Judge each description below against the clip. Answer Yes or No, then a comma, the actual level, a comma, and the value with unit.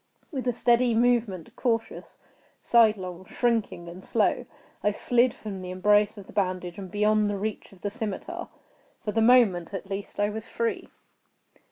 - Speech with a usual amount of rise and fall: Yes, average, 3.4 semitones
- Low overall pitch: No, high, 210 Hz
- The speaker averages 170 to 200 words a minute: No, average, 155 wpm